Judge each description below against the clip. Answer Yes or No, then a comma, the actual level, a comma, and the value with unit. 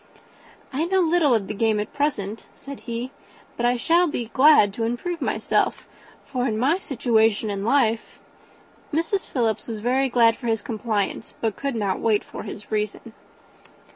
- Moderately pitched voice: No, high, 235 Hz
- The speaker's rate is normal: Yes, average, 170 wpm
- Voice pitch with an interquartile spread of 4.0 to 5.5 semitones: Yes, average, 4.3 semitones